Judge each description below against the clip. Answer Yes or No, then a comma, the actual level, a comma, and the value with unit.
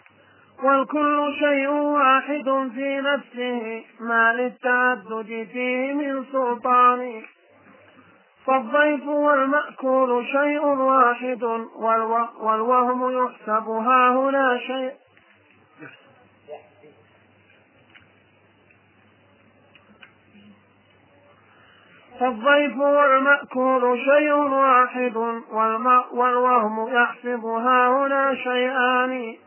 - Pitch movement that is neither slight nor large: Yes, average, 3.2 semitones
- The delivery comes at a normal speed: No, slow, 55 wpm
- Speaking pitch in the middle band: No, very high, 250 Hz